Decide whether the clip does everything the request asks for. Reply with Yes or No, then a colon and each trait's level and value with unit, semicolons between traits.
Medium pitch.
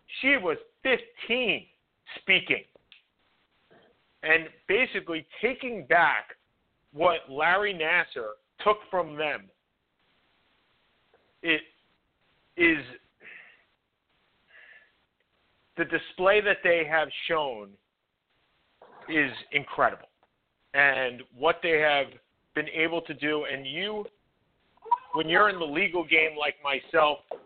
Yes: medium, 160 Hz